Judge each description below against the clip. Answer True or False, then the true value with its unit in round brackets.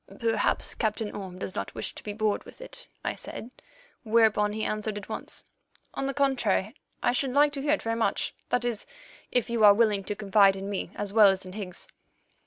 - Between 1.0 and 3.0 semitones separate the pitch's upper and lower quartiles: True (2.7 semitones)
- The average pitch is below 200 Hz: False (215 Hz)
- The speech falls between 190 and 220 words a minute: True (205 wpm)